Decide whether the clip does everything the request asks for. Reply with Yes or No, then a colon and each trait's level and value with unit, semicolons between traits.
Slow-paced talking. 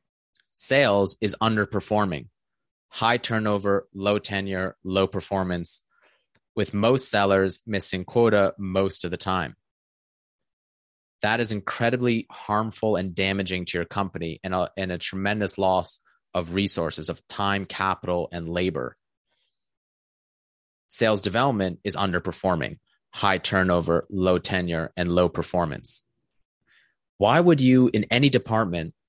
Yes: slow, 120 wpm